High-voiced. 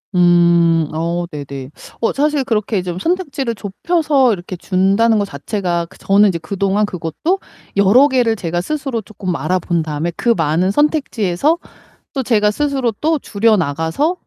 Yes: high, 200 Hz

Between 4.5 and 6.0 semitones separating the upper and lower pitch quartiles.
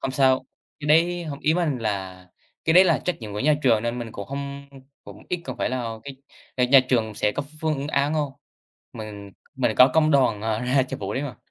Yes: average, 5.0 semitones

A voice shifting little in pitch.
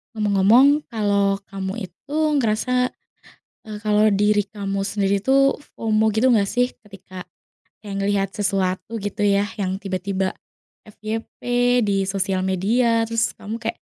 Yes: narrow, 2.3 semitones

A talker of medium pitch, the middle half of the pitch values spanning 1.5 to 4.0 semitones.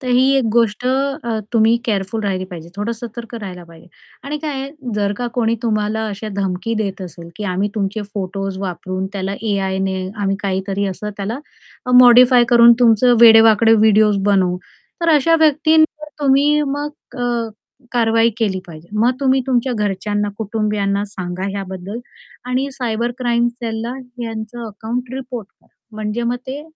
No: high, 220 Hz; average, 3.7 semitones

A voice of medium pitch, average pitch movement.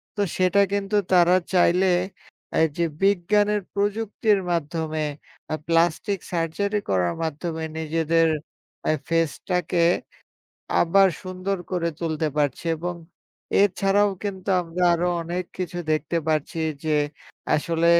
Yes: medium, 175 Hz; average, 3.2 semitones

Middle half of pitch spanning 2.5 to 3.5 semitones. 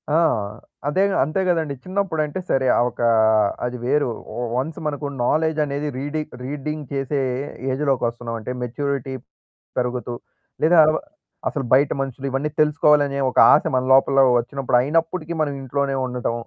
Yes: average, 2.8 semitones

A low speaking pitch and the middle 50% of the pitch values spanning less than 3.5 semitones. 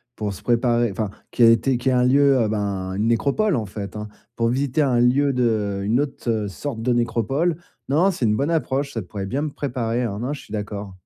No: low, 120 Hz; average, 4.3 semitones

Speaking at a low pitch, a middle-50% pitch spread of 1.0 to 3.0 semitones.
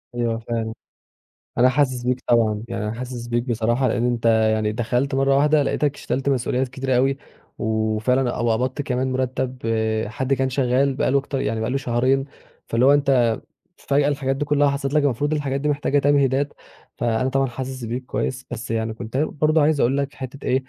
Yes: low, 130 Hz; narrow, 2.6 semitones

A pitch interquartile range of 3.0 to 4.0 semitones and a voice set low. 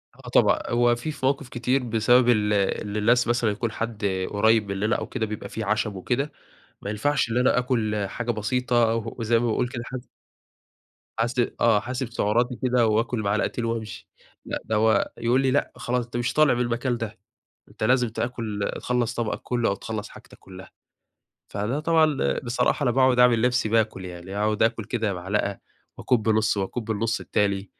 No: narrow, 2.6 semitones; low, 115 Hz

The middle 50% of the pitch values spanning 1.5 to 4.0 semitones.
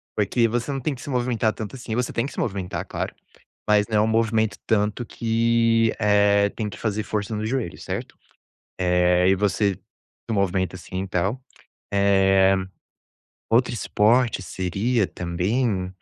Yes: average, 3.1 semitones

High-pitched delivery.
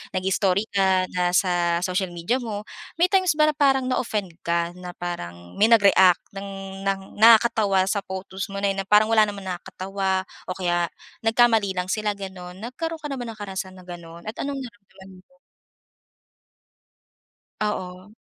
Yes: high, 195 Hz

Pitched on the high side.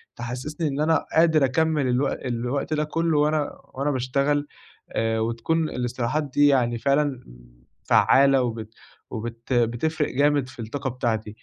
No: low, 135 Hz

